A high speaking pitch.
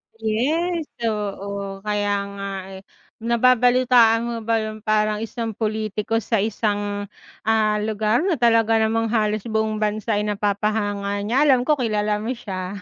Yes: high, 215 Hz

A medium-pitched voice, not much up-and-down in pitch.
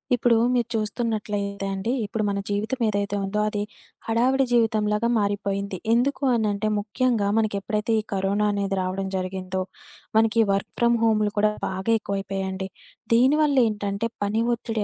No: high, 210 Hz; narrow, 2.3 semitones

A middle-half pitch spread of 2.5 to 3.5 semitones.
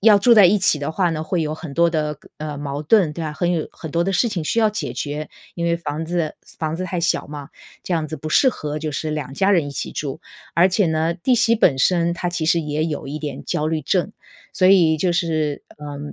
Yes: average, 2.8 semitones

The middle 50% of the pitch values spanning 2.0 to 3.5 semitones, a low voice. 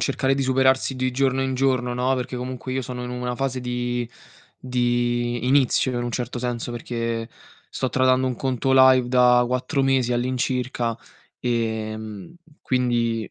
No: narrow, 1.3 semitones; low, 125 Hz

